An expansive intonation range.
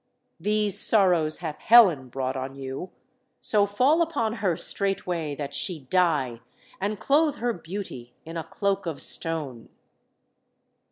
Yes: wide, 6.3 semitones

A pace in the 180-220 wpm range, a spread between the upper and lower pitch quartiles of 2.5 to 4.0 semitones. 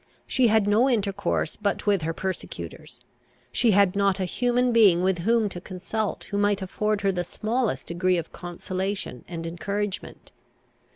No: average, 160 wpm; average, 2.8 semitones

